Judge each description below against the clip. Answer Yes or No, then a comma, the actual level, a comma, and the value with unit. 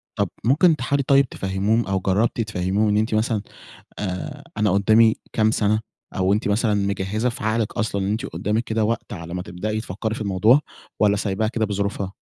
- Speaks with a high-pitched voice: No, low, 105 Hz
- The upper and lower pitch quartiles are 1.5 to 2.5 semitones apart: Yes, narrow, 2.2 semitones